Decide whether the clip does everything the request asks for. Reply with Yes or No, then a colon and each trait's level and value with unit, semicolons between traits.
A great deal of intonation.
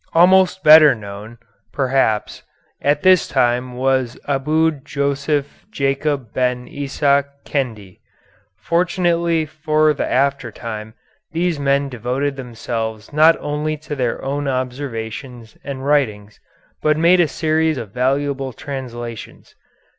No: average, 3.7 semitones